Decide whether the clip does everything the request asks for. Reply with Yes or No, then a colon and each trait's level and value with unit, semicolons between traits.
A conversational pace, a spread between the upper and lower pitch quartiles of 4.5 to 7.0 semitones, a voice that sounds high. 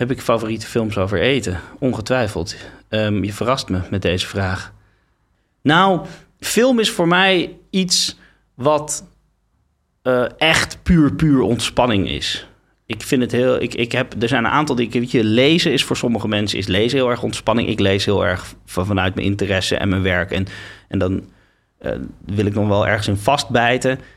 No: average, 180 wpm; average, 4.9 semitones; low, 115 Hz